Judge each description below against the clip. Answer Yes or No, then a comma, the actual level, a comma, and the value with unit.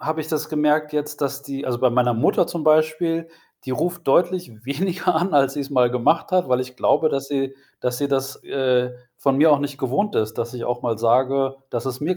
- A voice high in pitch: No, medium, 140 Hz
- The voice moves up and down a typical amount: Yes, average, 3.6 semitones